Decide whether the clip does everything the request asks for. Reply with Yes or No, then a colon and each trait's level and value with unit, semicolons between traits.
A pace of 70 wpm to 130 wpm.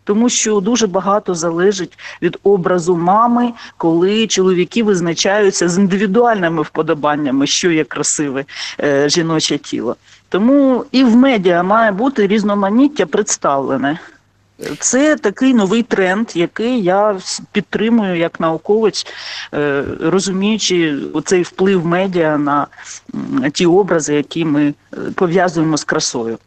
Yes: average, 110 wpm